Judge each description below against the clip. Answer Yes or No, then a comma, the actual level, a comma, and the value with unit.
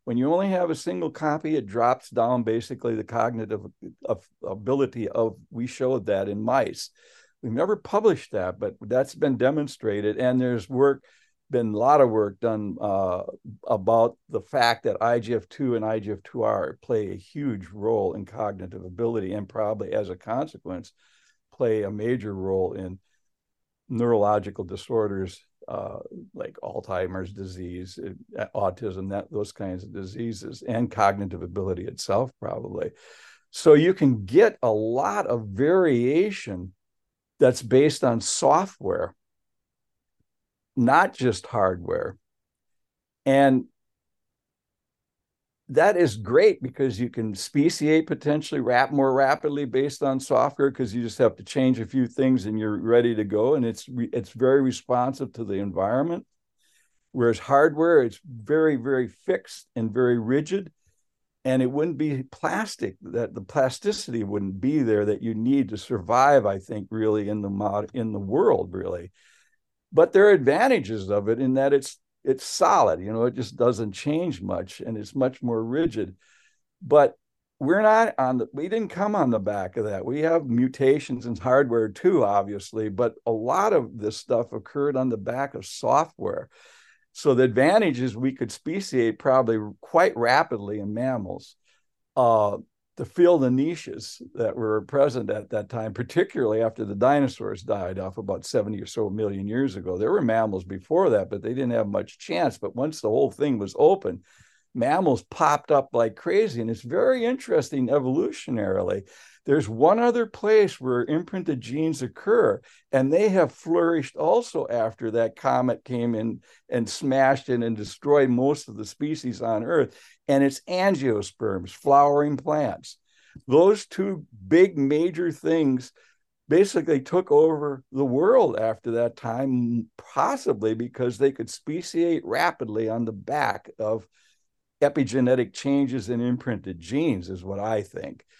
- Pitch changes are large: No, average, 4.7 semitones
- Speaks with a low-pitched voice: Yes, low, 125 Hz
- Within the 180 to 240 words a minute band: No, average, 155 wpm